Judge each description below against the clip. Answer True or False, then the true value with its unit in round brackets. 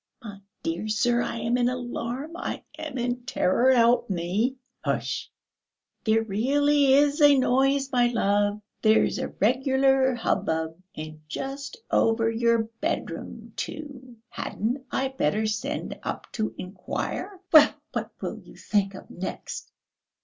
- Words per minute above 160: False (135 wpm)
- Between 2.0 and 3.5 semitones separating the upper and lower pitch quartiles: False (4.1 semitones)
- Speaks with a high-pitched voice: True (240 Hz)